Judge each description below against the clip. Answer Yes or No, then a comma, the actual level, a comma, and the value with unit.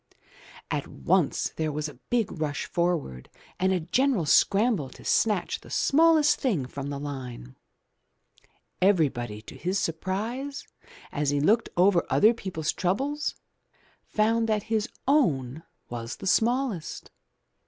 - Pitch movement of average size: No, wide, 7.8 semitones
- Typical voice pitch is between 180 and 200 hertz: Yes, medium, 185 Hz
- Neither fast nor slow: No, slow, 130 wpm